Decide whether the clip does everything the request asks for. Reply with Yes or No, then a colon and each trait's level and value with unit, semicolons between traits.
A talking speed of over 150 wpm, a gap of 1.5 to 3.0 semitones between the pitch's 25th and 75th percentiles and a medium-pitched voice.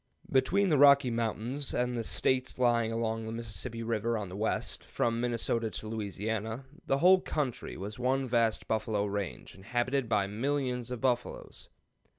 No: average, 160 wpm; average, 2.7 semitones; low, 115 Hz